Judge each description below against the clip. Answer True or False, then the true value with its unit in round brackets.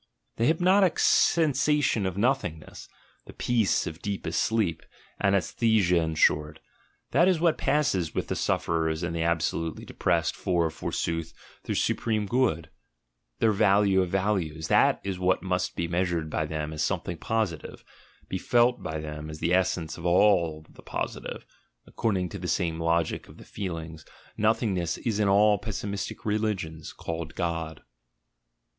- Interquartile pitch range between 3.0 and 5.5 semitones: True (4.6 semitones)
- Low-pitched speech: True (90 Hz)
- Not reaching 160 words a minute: True (150 wpm)